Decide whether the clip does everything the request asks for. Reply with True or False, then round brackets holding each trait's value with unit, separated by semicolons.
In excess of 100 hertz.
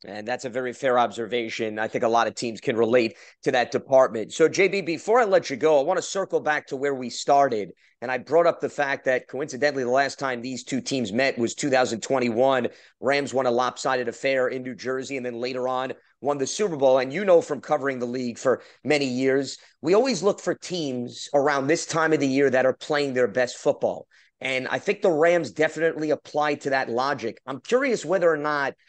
True (135 Hz)